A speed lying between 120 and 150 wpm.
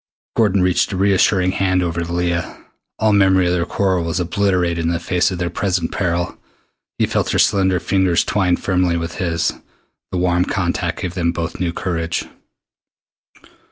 No: average, 170 wpm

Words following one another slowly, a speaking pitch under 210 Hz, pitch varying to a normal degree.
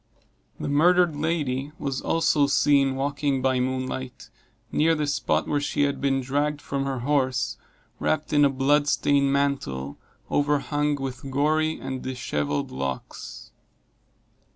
No: slow, 130 wpm; medium, 140 Hz; narrow, 2.1 semitones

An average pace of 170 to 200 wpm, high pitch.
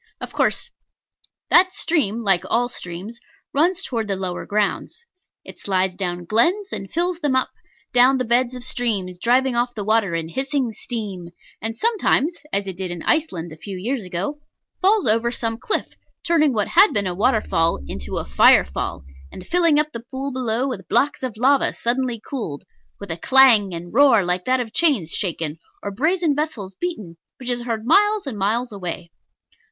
Yes: average, 185 wpm; high, 235 Hz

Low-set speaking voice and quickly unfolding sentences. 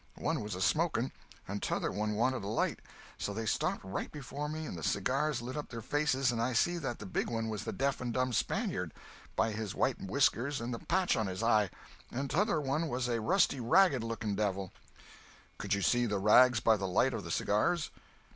Yes: low, 120 Hz; fast, 215 wpm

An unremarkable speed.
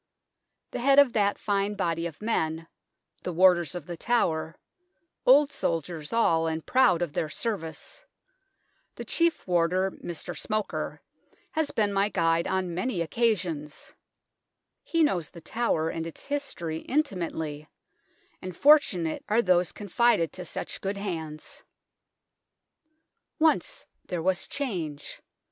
No: slow, 130 wpm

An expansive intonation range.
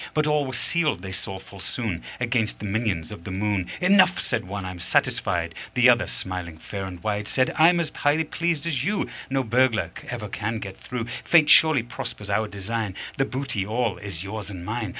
Yes: wide, 5.7 semitones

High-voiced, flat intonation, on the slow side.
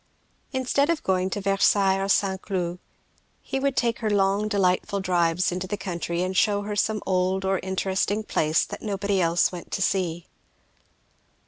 No: high, 195 Hz; narrow, 2.1 semitones; average, 165 wpm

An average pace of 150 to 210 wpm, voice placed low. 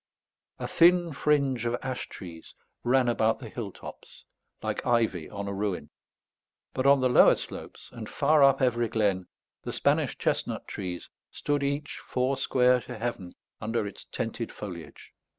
Yes: average, 155 wpm; low, 120 Hz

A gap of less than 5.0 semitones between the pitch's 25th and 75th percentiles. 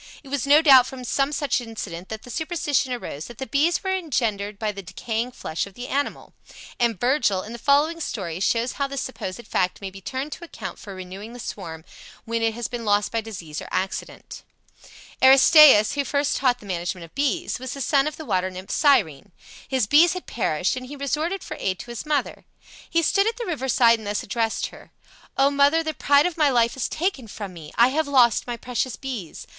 No: wide, 5.6 semitones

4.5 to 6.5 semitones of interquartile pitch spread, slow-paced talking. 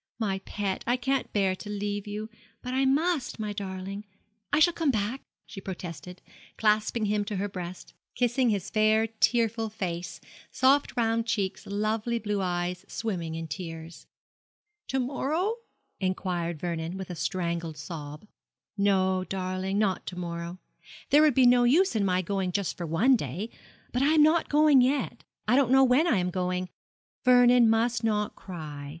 No: average, 5.1 semitones; average, 165 wpm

